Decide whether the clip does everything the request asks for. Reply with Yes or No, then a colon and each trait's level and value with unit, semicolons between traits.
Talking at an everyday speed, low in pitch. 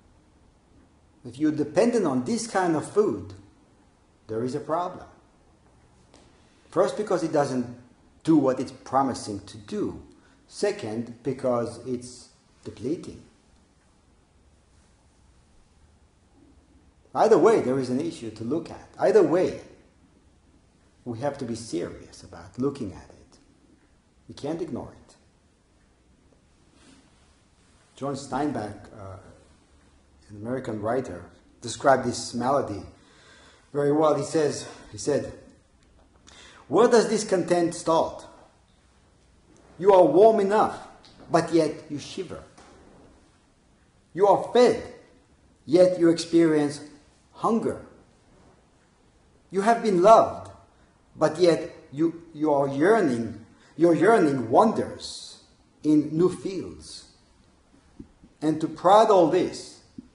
No: slow, 105 wpm; low, 125 Hz